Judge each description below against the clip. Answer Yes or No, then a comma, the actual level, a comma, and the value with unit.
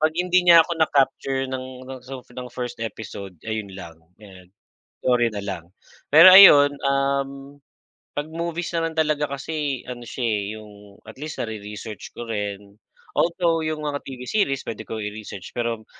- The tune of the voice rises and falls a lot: Yes, wide, 5.7 semitones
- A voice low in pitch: Yes, low, 130 Hz